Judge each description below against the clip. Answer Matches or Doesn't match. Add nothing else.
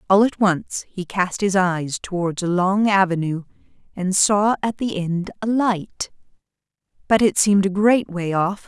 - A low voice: Doesn't match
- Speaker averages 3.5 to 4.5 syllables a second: Matches